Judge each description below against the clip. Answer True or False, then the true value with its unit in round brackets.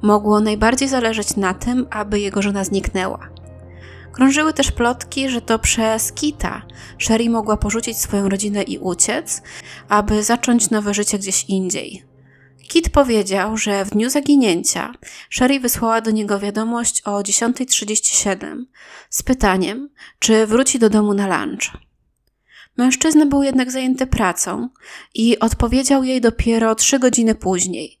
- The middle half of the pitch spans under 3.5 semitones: False (3.9 semitones)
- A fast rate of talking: False (135 wpm)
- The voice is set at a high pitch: True (220 Hz)